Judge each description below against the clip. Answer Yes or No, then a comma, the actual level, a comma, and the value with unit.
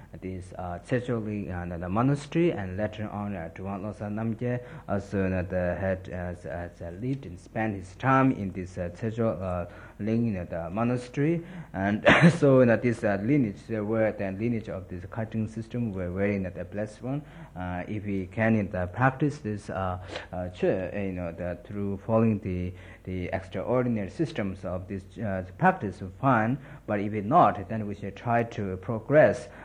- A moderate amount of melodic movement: Yes, average, 4.1 semitones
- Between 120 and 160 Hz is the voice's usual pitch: No, low, 105 Hz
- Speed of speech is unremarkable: No, fast, 175 wpm